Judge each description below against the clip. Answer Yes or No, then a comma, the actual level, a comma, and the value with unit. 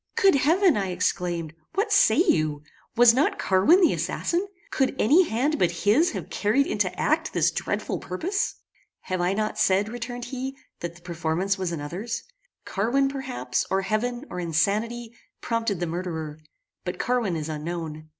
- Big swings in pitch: Yes, wide, 7.2 semitones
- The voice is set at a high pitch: Yes, high, 210 Hz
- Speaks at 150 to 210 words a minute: Yes, average, 160 wpm